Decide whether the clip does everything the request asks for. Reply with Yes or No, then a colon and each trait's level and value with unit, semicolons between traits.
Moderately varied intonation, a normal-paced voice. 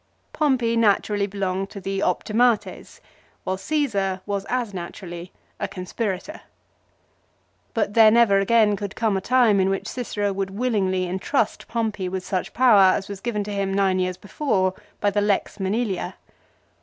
Yes: average, 3.0 semitones; average, 155 wpm